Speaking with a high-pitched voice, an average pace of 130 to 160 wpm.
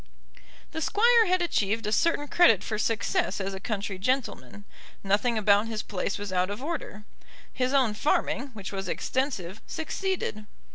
Yes: high, 215 Hz; average, 155 wpm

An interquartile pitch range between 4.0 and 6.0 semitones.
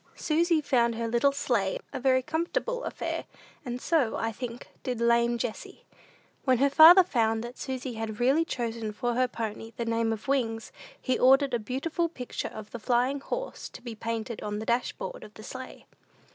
No: average, 3.4 semitones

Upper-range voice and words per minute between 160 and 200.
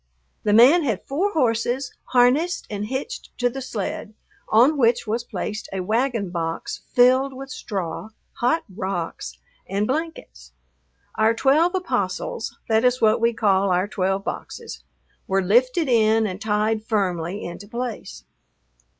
No: high, 225 Hz; average, 140 wpm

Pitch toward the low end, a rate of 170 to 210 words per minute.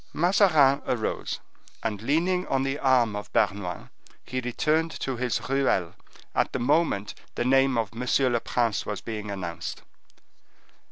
No: low, 125 Hz; average, 145 wpm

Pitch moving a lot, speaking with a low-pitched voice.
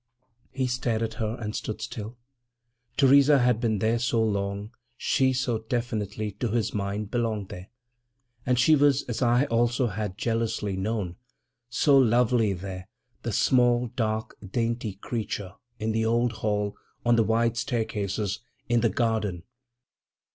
No: narrow, 2.5 semitones; low, 115 Hz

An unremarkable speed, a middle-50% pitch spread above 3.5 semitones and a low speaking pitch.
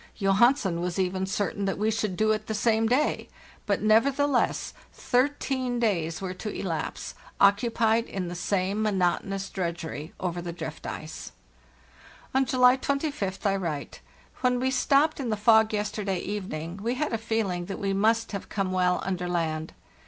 No: average, 160 wpm; average, 4.1 semitones; high, 205 Hz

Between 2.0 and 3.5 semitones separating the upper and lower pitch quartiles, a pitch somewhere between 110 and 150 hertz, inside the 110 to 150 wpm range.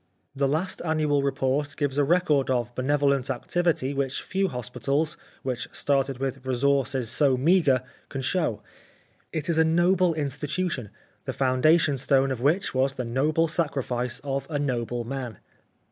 Yes: average, 3.2 semitones; medium, 140 Hz; average, 145 wpm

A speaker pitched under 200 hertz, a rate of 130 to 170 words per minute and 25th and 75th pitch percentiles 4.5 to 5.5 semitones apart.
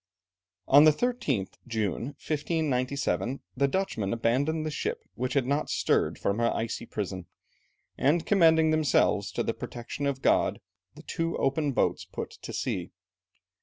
Yes: medium, 140 Hz; average, 145 wpm; average, 5.1 semitones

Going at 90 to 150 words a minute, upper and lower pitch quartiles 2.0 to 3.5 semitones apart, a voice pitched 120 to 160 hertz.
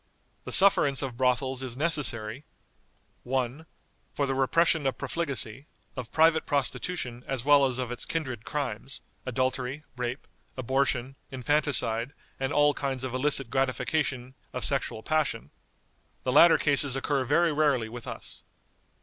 Yes: slow, 135 wpm; narrow, 2.6 semitones; low, 135 Hz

